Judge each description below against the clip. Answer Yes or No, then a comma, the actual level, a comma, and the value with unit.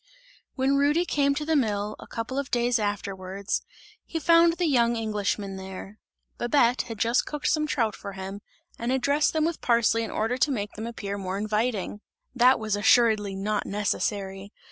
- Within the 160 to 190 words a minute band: Yes, average, 180 wpm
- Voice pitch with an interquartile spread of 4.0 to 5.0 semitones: Yes, average, 4.7 semitones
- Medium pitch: No, high, 225 Hz